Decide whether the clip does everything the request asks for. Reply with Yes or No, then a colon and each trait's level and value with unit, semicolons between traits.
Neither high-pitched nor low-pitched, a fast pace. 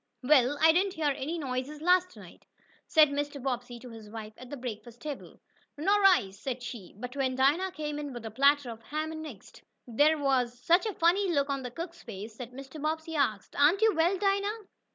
No: very high, 285 Hz; fast, 210 wpm